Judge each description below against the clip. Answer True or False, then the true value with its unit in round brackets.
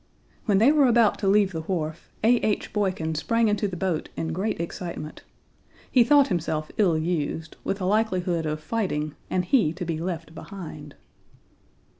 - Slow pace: False (170 wpm)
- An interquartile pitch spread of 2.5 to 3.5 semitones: False (4.7 semitones)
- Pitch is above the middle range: False (180 Hz)